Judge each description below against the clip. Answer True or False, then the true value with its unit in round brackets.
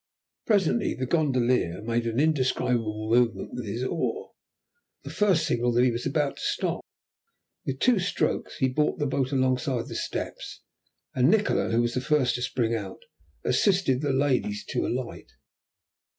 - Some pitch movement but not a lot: True (4.2 semitones)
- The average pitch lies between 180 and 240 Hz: False (130 Hz)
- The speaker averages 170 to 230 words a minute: False (160 wpm)